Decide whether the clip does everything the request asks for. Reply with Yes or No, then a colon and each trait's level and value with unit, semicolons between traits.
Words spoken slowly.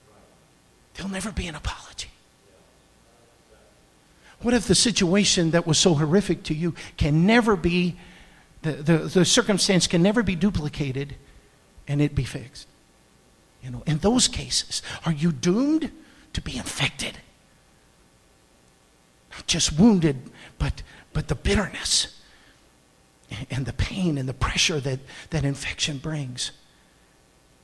Yes: slow, 130 wpm